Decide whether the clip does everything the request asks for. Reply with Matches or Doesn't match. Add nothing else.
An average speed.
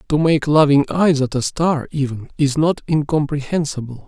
Matches